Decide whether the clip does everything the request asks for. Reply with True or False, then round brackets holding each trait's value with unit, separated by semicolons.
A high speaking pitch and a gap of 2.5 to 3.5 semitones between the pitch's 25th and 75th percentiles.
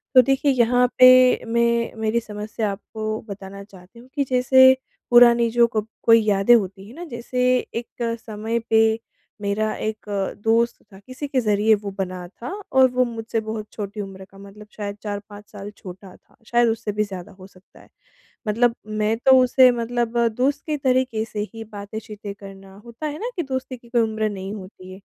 True (220 Hz; 2.9 semitones)